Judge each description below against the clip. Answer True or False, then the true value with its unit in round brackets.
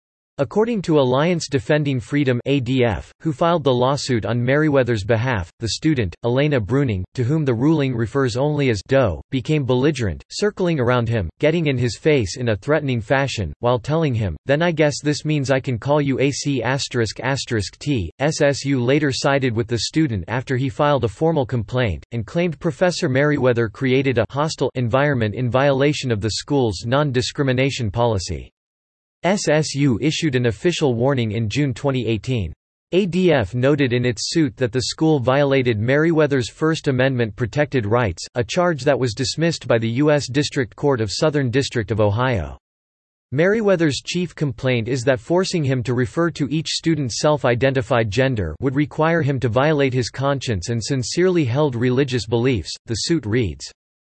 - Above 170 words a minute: False (160 wpm)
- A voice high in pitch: False (135 Hz)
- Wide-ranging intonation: False (3.8 semitones)